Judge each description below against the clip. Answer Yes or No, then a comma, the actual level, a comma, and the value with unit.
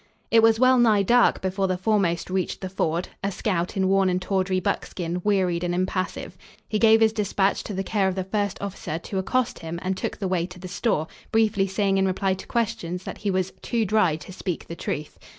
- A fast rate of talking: Yes, fast, 220 wpm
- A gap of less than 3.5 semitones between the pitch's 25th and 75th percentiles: Yes, narrow, 2.4 semitones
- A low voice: No, high, 190 Hz